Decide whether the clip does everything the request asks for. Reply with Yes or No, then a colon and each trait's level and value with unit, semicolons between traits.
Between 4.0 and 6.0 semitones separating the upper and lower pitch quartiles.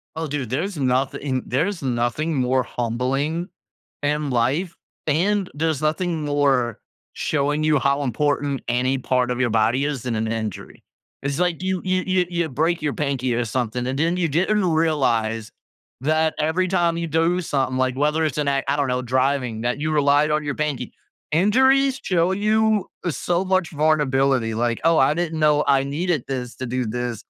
Yes: average, 4.4 semitones